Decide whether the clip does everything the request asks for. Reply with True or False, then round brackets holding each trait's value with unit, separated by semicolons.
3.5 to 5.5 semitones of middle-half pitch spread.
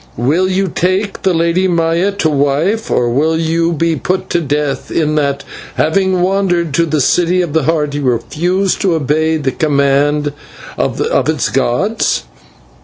True (3.8 semitones)